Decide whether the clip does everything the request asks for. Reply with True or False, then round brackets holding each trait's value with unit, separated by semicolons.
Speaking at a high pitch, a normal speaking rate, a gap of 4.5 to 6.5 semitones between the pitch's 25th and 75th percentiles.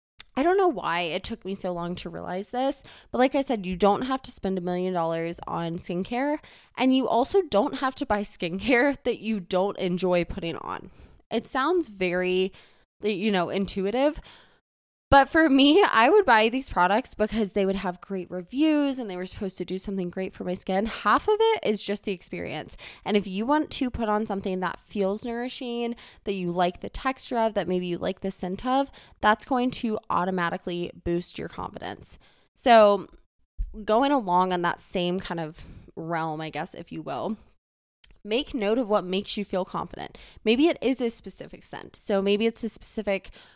True (205 Hz; 195 wpm; 5.2 semitones)